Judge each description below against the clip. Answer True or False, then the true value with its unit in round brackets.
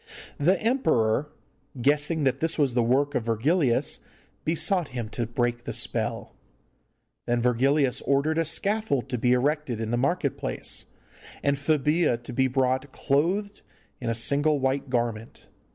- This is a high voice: False (135 Hz)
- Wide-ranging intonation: False (4.2 semitones)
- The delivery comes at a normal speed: True (150 wpm)